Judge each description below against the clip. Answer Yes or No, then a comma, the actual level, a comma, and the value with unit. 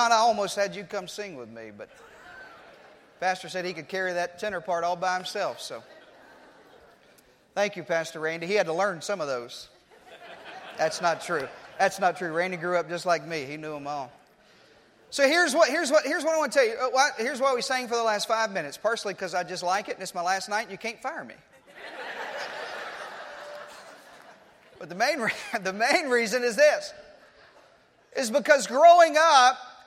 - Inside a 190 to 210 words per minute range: Yes, average, 195 wpm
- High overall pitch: Yes, high, 205 Hz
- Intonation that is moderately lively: No, wide, 6.3 semitones